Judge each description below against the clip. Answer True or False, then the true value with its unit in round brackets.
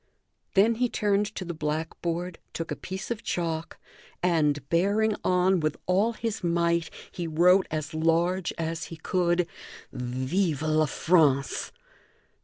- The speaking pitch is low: False (170 Hz)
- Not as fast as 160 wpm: True (135 wpm)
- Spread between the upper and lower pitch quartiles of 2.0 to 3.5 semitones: True (2.9 semitones)